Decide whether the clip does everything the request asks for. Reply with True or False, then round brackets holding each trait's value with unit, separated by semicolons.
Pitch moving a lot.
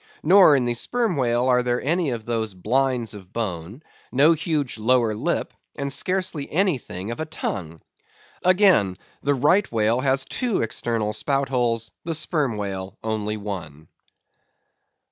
True (5.7 semitones)